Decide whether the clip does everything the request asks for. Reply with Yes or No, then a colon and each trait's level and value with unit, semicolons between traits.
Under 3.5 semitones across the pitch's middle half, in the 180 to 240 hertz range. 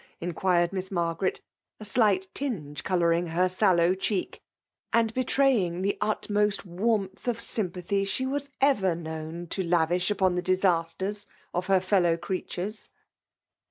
Yes: average, 3.1 semitones; medium, 185 Hz